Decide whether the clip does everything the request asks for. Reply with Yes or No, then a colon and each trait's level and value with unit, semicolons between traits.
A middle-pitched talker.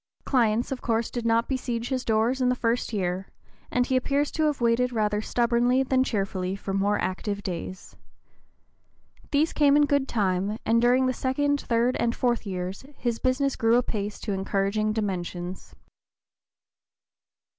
No: high, 230 Hz